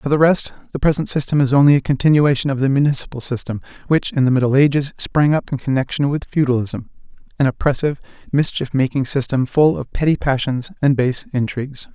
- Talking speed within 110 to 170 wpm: No, average, 180 wpm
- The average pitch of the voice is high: No, medium, 140 Hz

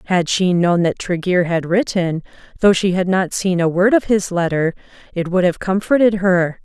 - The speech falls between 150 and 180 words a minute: No, average, 200 wpm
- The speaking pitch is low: No, medium, 185 Hz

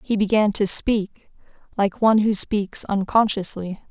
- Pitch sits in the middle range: No, high, 205 Hz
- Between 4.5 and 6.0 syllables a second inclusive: No, 4.3 syllables/s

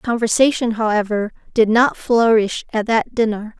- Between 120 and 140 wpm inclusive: Yes, slow, 135 wpm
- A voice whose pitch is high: Yes, high, 225 Hz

